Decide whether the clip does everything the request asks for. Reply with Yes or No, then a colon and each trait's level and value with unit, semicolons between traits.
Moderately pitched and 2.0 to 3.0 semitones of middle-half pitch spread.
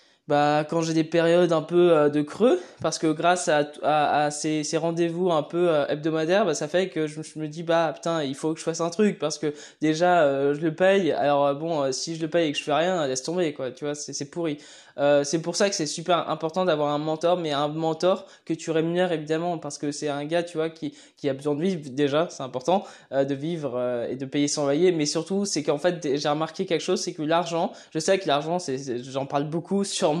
Yes: medium, 160 Hz; average, 2.7 semitones